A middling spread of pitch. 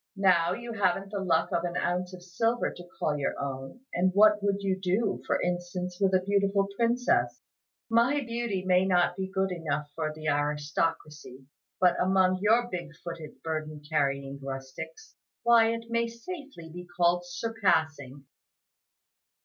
Yes: average, 4.2 semitones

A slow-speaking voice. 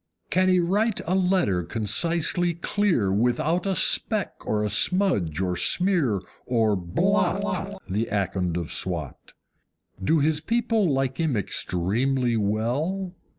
Yes: slow, 125 wpm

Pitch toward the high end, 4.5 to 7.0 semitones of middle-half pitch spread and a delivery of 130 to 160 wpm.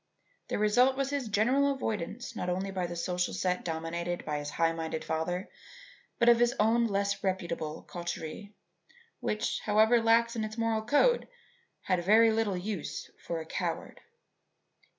Yes: high, 205 Hz; average, 4.8 semitones; average, 155 wpm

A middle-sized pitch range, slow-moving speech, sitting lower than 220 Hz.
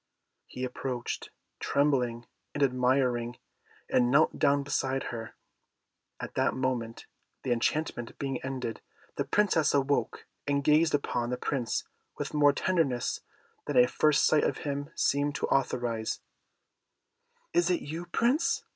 Yes: average, 3.2 semitones; slow, 130 wpm; low, 135 Hz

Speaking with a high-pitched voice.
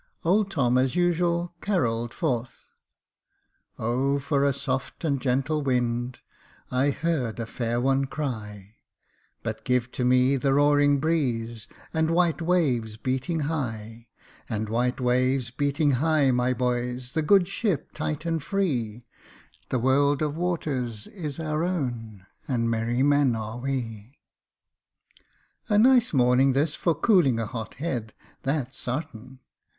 No: low, 130 Hz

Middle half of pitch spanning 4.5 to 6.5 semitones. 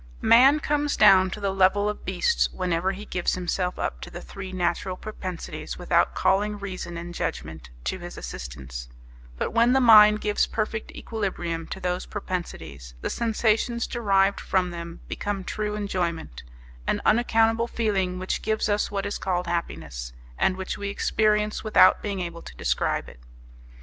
No: average, 3.6 semitones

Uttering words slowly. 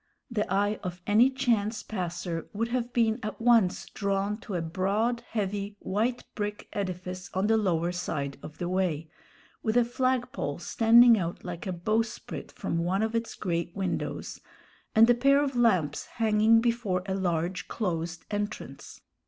No: average, 160 wpm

